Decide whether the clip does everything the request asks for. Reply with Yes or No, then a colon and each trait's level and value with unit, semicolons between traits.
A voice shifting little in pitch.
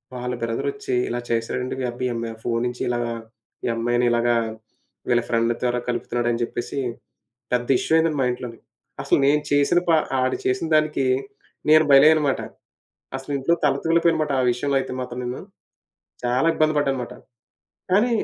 No: average, 3.5 semitones